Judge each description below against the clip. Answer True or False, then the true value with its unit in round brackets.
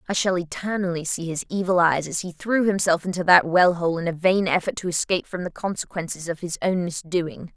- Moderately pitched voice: True (175 Hz)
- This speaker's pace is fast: True (220 wpm)